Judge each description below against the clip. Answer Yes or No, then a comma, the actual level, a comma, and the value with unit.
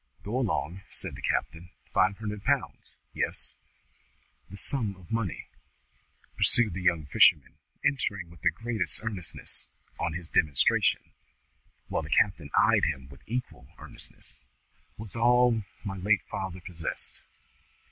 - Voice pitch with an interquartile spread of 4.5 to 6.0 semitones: Yes, average, 4.8 semitones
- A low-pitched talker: Yes, very low, 95 Hz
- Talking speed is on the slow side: Yes, slow, 130 wpm